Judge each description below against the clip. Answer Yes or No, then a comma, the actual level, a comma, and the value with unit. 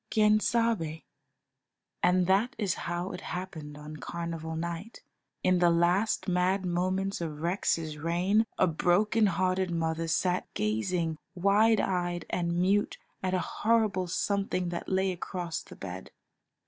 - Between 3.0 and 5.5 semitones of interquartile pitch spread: No, narrow, 2.6 semitones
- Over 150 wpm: No, slow, 135 wpm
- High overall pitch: No, medium, 180 Hz